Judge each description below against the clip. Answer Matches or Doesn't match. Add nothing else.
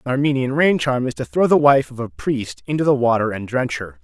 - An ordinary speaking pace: Doesn't match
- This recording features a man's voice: Matches